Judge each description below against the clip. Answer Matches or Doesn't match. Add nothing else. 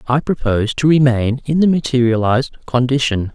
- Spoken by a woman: Doesn't match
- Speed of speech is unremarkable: Matches